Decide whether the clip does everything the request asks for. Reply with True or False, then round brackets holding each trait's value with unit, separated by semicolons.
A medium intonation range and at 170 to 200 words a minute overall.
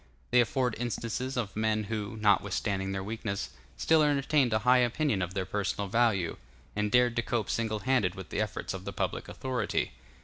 True (3.7 semitones; 180 wpm)